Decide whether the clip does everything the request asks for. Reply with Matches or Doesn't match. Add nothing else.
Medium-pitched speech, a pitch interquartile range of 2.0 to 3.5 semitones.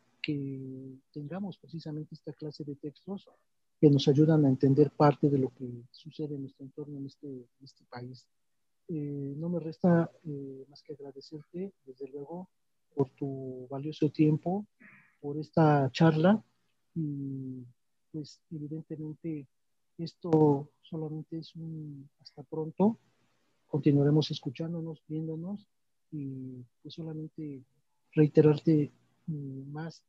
Matches